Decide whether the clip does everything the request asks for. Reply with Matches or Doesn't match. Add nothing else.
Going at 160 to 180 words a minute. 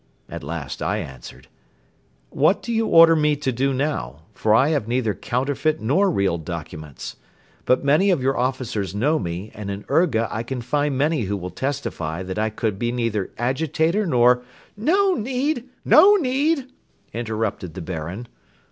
Matches